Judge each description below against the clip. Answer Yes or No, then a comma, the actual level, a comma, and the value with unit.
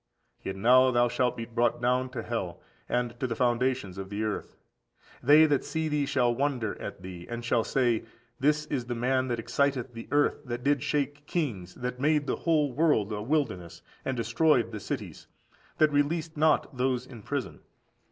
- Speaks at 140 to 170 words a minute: No, average, 185 wpm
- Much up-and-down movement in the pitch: No, average, 3.7 semitones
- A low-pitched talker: Yes, low, 125 Hz